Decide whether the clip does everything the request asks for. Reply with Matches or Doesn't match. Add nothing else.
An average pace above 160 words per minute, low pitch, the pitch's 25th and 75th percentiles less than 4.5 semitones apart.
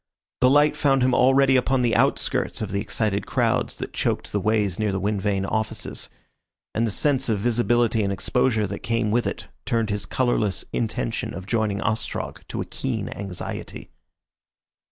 Matches